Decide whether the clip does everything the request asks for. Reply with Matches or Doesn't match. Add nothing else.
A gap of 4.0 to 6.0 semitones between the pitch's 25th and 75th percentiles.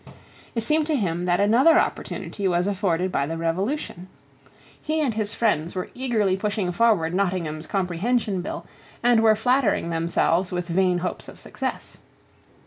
Matches